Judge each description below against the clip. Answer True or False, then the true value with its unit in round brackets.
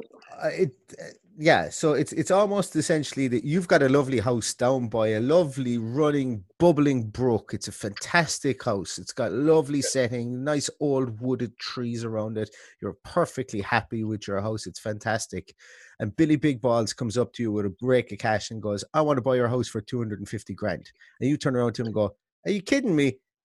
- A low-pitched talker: True (125 Hz)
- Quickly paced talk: True (210 wpm)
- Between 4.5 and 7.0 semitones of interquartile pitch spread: True (4.8 semitones)